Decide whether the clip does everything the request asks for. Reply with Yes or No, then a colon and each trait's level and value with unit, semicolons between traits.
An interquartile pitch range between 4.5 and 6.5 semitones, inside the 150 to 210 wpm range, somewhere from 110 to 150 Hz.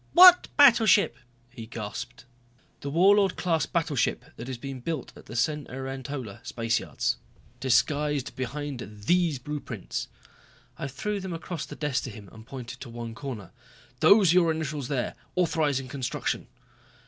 No: average, 5.1 semitones; average, 140 wpm; medium, 140 Hz